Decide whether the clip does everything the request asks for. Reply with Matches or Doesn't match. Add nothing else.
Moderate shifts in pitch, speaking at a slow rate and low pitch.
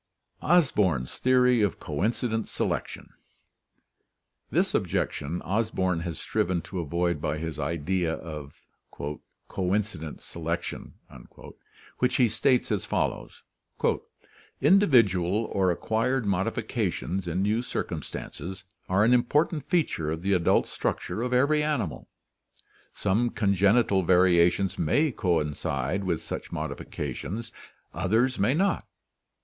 Doesn't match